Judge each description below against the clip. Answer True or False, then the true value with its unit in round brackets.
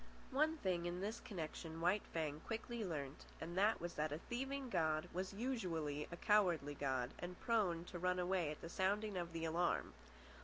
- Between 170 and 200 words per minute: True (185 wpm)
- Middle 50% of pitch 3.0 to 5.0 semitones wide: True (4.6 semitones)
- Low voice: False (175 Hz)